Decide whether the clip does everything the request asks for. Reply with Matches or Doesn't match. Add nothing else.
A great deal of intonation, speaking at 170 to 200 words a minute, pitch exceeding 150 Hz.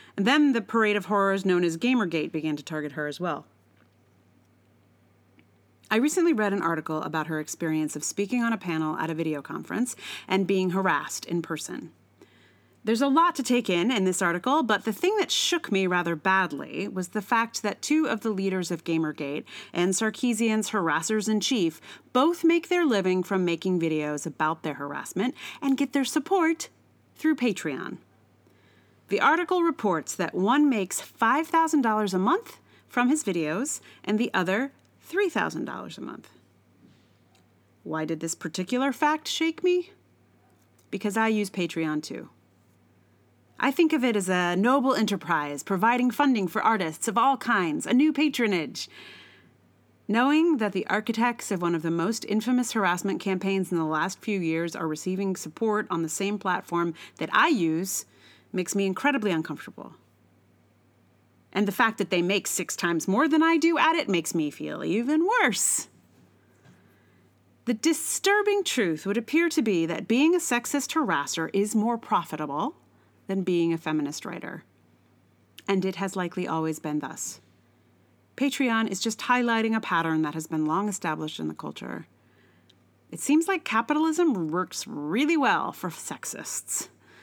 Doesn't match